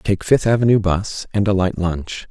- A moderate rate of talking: No, fast, 210 wpm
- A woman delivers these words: No, male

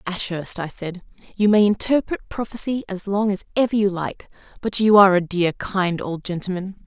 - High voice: Yes, high, 195 Hz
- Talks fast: No, average, 185 wpm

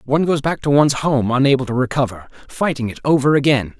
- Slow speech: No, fast, 205 wpm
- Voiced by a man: Yes, male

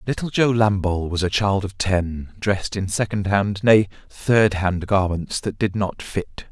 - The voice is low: Yes, low, 100 Hz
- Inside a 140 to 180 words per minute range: Yes, average, 175 wpm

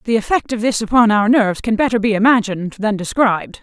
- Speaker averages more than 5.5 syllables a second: Yes, 6.4 syllables/s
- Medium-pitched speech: No, high, 220 Hz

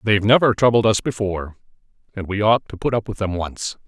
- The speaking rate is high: Yes, fast, 230 wpm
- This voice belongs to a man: Yes, male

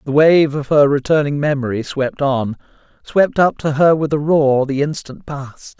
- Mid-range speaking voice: Yes, medium, 145 Hz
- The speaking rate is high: No, average, 175 wpm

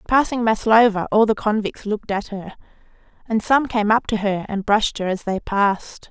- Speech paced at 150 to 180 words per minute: No, average, 195 wpm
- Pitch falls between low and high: No, high, 215 Hz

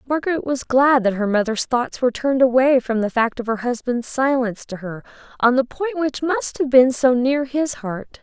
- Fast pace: Yes, fast, 220 wpm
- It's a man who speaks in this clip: No, female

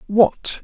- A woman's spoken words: No, male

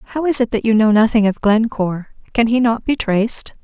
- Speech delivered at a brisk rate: Yes, fast, 215 wpm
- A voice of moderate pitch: No, high, 225 Hz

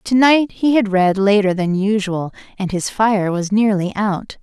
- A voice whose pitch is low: No, high, 205 Hz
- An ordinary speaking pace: Yes, average, 190 wpm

